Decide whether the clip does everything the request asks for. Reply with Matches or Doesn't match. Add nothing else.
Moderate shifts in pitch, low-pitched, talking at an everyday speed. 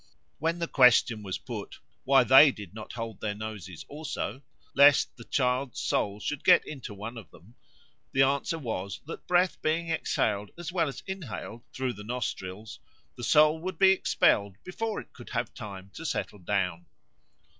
Doesn't match